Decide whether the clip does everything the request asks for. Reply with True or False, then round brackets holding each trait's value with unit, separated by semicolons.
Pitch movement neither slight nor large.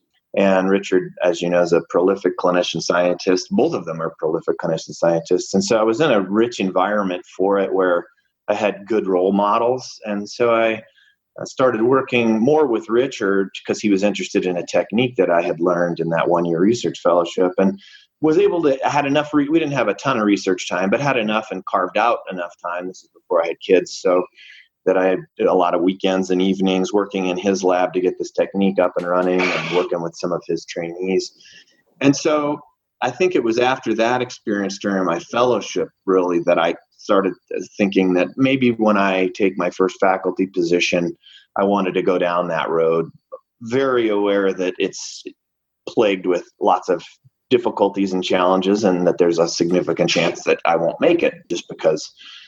True (3.6 semitones)